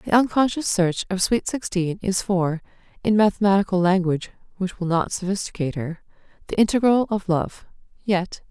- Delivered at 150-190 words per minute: No, average, 140 wpm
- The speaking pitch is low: No, high, 190 Hz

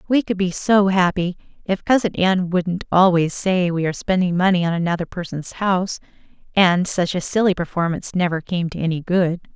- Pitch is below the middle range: No, medium, 180 Hz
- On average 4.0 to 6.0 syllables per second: Yes, 5.4 syllables/s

